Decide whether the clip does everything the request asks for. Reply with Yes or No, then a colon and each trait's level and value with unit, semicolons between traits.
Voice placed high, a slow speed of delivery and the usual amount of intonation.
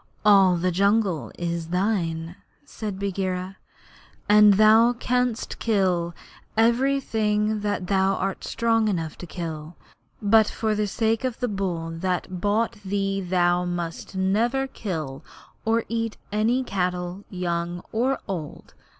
Yes: high, 195 Hz; slow, 125 wpm; average, 3.8 semitones